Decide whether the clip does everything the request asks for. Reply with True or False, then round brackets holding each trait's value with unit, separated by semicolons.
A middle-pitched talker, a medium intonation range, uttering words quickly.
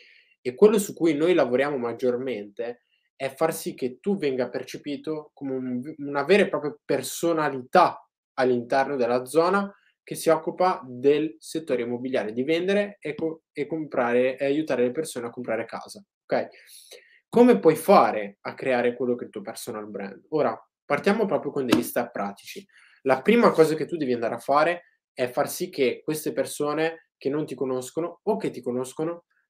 True (150 Hz; 4.8 semitones; 175 wpm)